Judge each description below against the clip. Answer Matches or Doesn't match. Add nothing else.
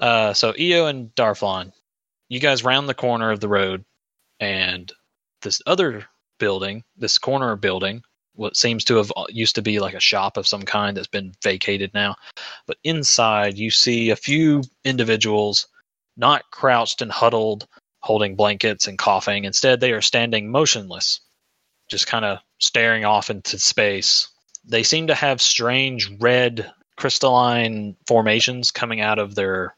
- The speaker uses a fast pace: Doesn't match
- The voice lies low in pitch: Matches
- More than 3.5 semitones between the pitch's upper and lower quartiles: Doesn't match